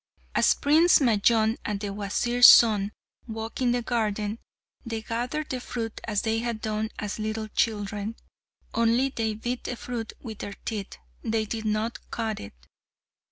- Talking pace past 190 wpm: No, average, 160 wpm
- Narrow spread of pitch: Yes, narrow, 1.9 semitones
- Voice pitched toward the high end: Yes, high, 225 Hz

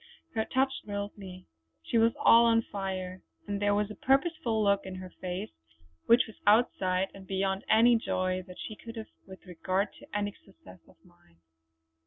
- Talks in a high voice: Yes, high, 200 Hz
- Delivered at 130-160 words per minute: No, average, 180 wpm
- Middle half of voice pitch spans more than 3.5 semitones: No, average, 3.2 semitones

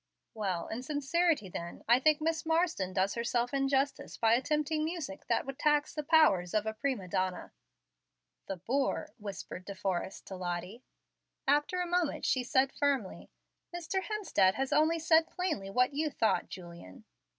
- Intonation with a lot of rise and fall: Yes, wide, 7.9 semitones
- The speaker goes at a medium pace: Yes, average, 160 wpm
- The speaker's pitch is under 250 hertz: No, very high, 270 Hz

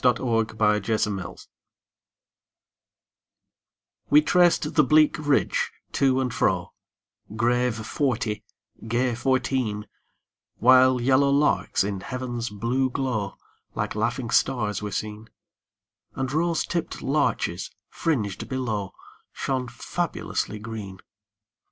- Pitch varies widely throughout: No, average, 3.7 semitones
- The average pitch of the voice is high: No, low, 125 Hz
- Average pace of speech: No, slow, 105 wpm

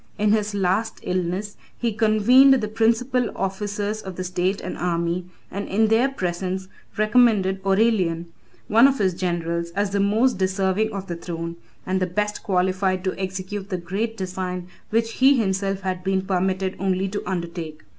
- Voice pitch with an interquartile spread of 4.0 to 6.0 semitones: No, narrow, 2.6 semitones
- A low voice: No, high, 195 Hz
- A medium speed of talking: Yes, average, 165 wpm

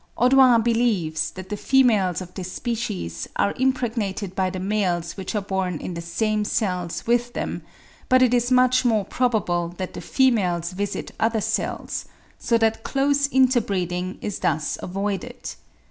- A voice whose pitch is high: Yes, high, 210 Hz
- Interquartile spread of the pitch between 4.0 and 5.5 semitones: Yes, average, 5.0 semitones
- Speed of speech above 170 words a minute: No, average, 160 wpm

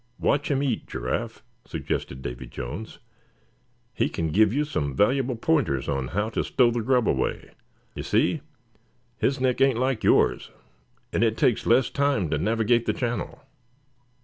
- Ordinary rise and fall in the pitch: No, wide, 8.2 semitones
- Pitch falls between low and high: No, low, 115 Hz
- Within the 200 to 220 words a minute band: No, average, 155 wpm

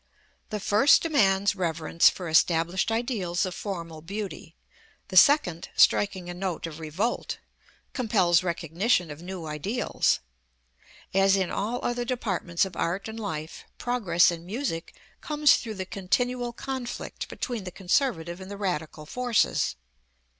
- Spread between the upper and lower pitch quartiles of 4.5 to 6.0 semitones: Yes, average, 5.1 semitones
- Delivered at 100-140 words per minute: Yes, slow, 135 wpm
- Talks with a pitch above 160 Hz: Yes, high, 190 Hz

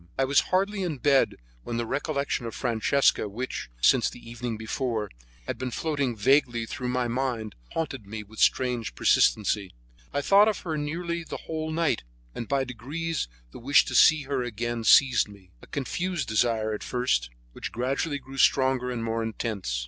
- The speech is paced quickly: No, average, 175 wpm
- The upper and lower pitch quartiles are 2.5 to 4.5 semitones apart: Yes, average, 4.0 semitones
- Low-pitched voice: Yes, low, 125 Hz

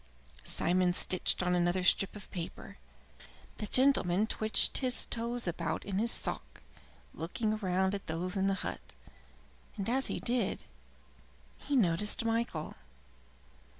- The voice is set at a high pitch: Yes, high, 195 Hz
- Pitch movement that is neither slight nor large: Yes, average, 4.3 semitones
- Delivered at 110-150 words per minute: Yes, slow, 135 wpm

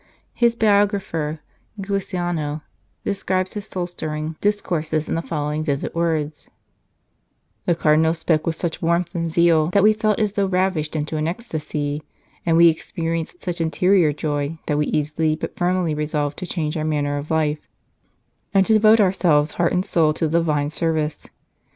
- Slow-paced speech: No, average, 165 wpm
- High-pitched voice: No, medium, 165 Hz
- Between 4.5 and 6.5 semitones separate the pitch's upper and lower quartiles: No, average, 3.1 semitones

